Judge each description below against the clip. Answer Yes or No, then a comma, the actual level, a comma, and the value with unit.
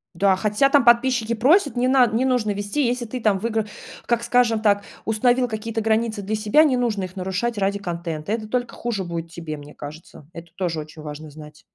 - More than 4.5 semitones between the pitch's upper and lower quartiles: Yes, average, 5.0 semitones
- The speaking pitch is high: Yes, high, 215 Hz